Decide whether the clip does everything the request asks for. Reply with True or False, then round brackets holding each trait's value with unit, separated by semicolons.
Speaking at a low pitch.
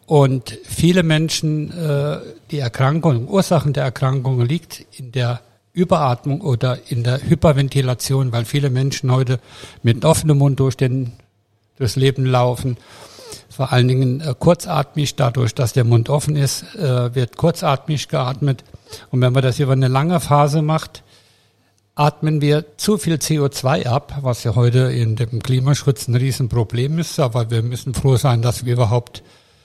True (130 Hz)